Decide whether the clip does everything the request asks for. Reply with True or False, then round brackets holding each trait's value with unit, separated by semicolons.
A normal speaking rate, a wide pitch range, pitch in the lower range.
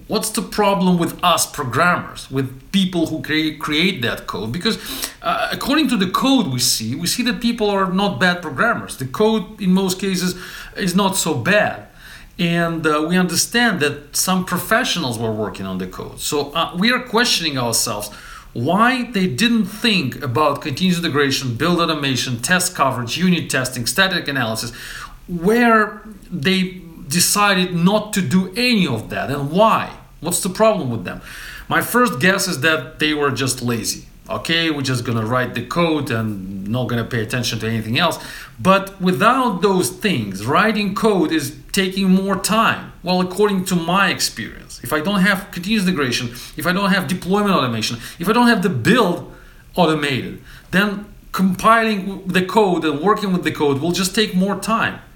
False (175 wpm; 6.0 semitones; 180 Hz)